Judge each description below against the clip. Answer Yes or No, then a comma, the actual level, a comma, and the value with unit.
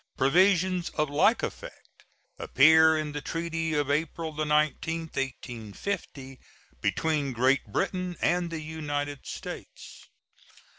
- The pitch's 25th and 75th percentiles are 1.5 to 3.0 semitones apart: Yes, narrow, 2.6 semitones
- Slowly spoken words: Yes, slow, 105 wpm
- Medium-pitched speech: Yes, medium, 155 Hz